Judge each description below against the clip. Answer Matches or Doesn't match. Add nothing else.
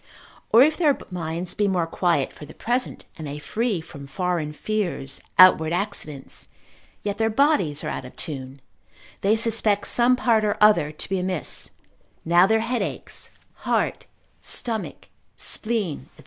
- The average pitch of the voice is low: Doesn't match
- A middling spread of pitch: Doesn't match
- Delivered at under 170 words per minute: Matches